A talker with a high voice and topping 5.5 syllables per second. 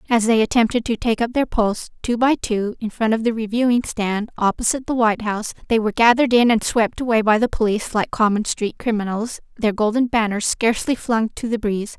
Yes: high, 225 Hz; 5.9 syllables/s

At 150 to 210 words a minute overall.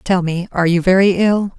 No: fast, 225 wpm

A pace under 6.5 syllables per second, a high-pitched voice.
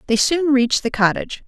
Yes: 6.2 syllables/s; very high, 260 Hz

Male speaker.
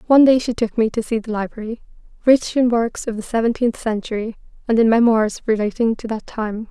No: female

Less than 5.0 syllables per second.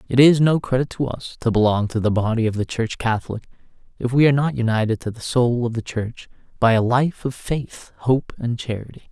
No: 5.6 syllables/s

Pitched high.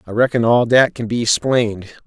No: low, 115 Hz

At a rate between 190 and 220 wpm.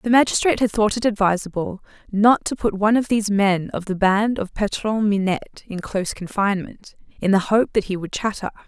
Yes: average, 200 wpm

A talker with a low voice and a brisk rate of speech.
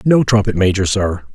No: low, 105 Hz; average, 180 wpm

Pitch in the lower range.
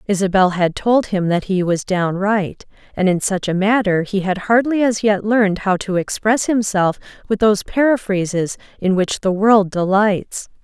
No: high, 200 Hz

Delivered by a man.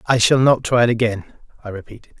Yes: male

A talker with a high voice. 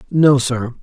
No: low, 130 Hz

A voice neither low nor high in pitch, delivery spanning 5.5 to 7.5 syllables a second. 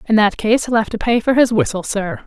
No: high, 220 Hz; 5.6 syllables/s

